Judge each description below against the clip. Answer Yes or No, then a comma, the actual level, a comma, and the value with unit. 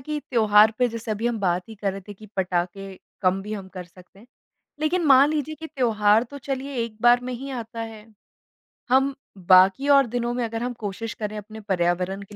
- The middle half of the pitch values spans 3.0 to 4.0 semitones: No, average, 4.4 semitones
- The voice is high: Yes, high, 225 Hz